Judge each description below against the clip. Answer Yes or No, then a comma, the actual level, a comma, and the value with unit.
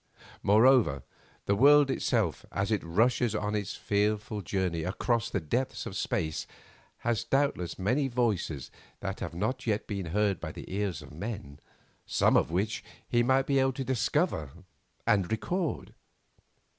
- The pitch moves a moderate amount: Yes, average, 5.0 semitones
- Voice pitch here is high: No, low, 105 Hz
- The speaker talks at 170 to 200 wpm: No, average, 150 wpm